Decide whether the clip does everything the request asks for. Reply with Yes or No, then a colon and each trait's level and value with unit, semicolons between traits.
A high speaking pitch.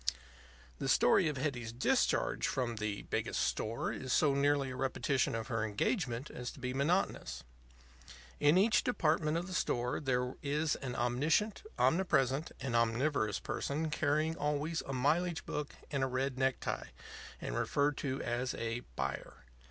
No: low, 135 Hz